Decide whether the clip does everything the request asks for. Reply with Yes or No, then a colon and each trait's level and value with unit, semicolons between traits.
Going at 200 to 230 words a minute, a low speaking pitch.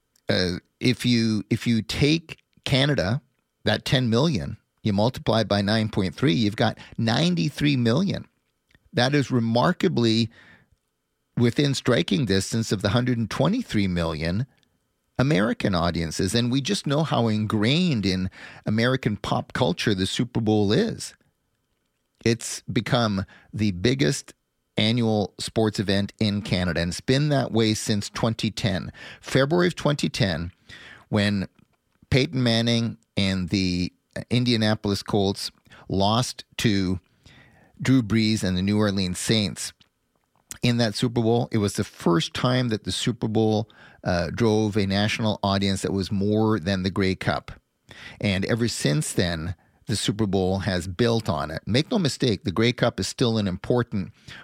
No: average, 140 wpm; low, 110 Hz